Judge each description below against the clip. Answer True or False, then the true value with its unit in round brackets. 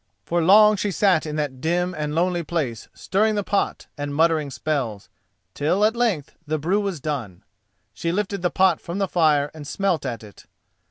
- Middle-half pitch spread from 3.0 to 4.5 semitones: False (4.9 semitones)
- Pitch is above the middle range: False (165 Hz)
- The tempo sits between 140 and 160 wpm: False (185 wpm)